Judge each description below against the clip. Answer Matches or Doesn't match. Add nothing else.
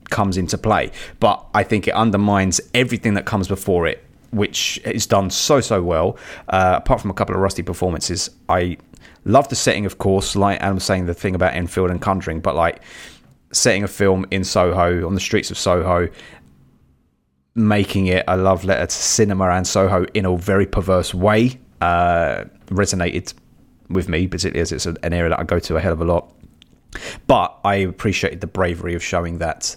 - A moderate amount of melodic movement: Doesn't match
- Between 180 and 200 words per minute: Matches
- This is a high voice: Doesn't match